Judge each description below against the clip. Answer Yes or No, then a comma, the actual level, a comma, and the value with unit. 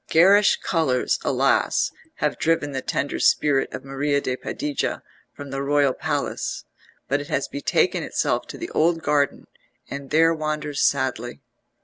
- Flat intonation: Yes, narrow, 2.1 semitones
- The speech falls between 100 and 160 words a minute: Yes, average, 145 wpm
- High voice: No, medium, 145 Hz